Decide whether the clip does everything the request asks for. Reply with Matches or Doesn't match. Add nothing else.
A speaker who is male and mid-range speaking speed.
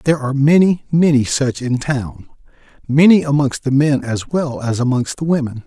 Matches